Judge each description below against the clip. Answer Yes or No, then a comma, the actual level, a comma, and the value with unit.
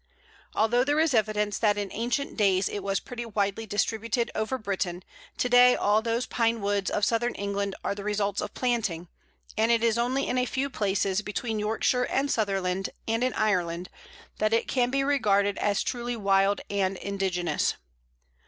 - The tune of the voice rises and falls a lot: No, average, 3.2 semitones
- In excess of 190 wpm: No, average, 175 wpm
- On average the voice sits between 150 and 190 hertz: No, high, 215 Hz